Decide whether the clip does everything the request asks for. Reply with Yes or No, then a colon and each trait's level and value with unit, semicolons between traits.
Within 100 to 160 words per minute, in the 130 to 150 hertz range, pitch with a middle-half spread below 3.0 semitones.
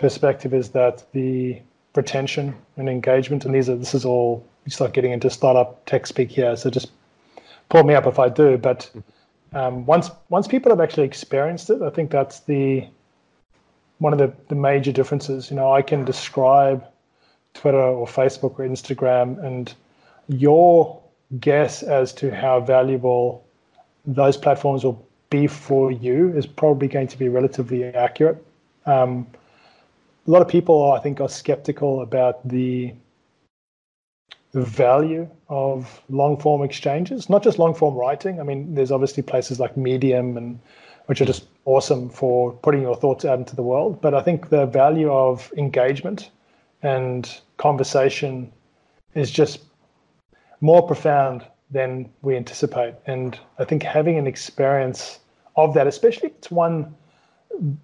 Yes: average, 150 wpm; low, 135 Hz; narrow, 2.5 semitones